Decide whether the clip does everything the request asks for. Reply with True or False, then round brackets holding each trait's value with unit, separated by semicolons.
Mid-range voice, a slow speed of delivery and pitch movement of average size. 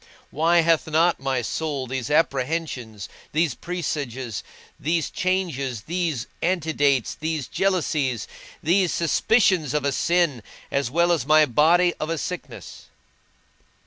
True (155 Hz; 120 wpm; 4.1 semitones)